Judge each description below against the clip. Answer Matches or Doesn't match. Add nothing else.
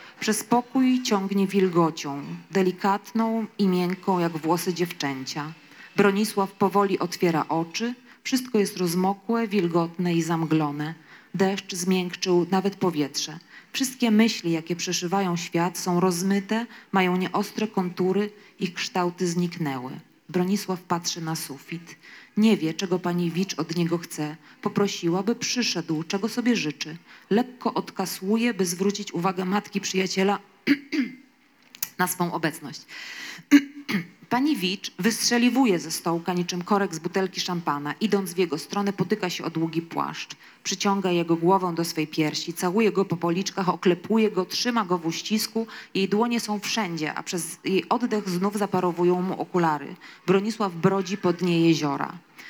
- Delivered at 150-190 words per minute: Doesn't match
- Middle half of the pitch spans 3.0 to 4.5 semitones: Matches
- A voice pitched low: Doesn't match